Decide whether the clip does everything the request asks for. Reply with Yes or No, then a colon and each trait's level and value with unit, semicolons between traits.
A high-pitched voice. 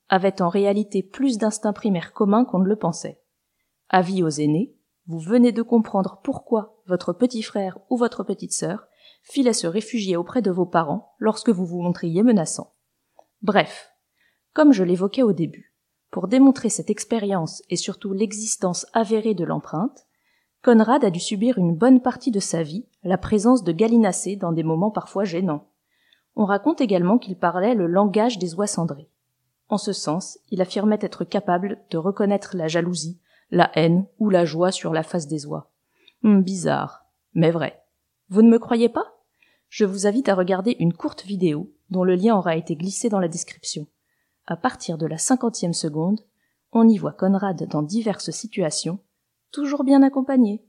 Yes: high, 200 Hz